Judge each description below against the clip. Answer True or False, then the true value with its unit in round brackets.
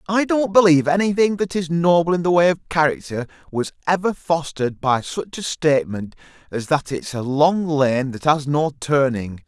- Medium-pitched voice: True (155 Hz)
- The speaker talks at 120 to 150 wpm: False (185 wpm)